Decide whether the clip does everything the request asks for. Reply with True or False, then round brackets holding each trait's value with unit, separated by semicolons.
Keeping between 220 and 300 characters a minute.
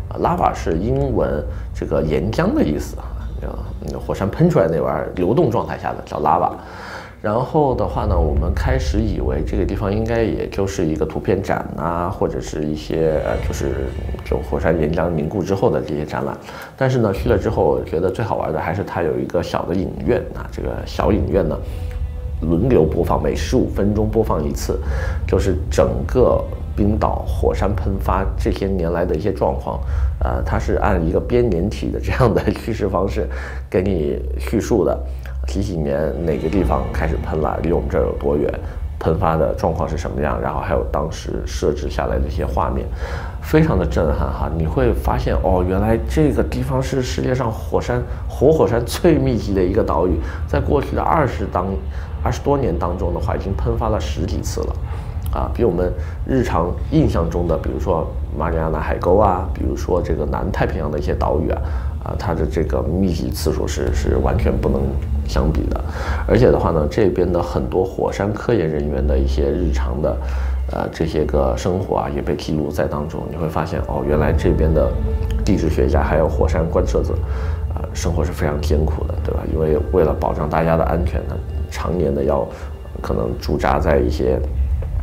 True (290 characters per minute)